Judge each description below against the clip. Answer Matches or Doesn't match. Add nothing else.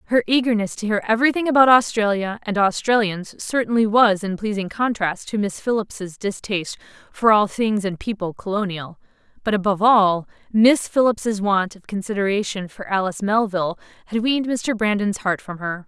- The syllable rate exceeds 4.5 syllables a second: Matches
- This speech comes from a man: Doesn't match